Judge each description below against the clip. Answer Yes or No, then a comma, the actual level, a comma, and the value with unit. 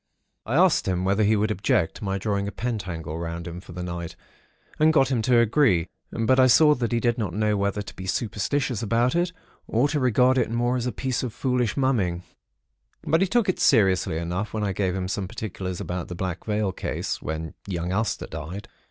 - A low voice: Yes, low, 105 Hz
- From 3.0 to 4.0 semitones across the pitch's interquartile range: No, average, 5.2 semitones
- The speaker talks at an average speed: No, fast, 215 wpm